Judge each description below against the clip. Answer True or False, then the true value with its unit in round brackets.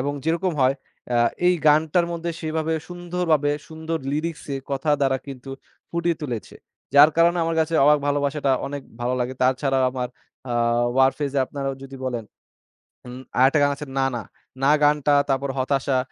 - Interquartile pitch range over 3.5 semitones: False (3.2 semitones)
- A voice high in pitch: False (145 Hz)